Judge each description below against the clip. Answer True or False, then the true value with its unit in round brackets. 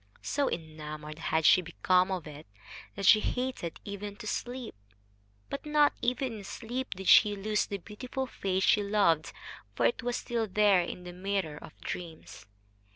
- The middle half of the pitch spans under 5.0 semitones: False (5.3 semitones)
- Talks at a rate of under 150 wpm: False (165 wpm)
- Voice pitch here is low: False (200 Hz)